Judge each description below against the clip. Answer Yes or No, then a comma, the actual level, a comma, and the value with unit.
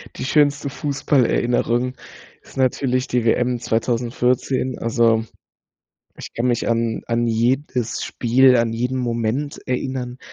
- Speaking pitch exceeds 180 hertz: No, low, 125 Hz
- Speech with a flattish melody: Yes, narrow, 2.0 semitones